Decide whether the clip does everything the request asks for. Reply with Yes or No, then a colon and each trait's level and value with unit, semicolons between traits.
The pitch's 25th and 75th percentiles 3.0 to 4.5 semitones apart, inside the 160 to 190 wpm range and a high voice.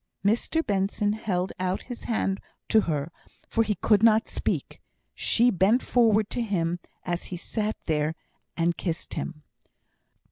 No: average, 4.1 semitones; average, 145 wpm; high, 200 Hz